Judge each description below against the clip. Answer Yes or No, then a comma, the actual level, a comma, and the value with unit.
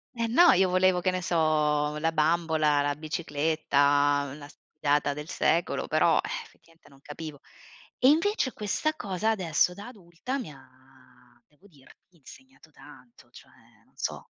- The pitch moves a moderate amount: Yes, average, 4.4 semitones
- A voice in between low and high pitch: Yes, medium, 160 Hz